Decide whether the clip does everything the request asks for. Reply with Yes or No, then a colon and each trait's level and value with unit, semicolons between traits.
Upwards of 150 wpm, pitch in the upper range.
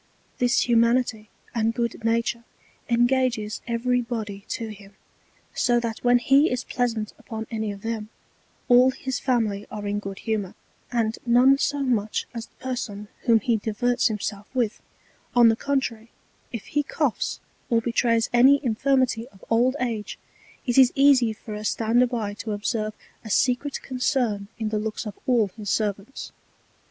Yes: average, 160 wpm; high, 230 Hz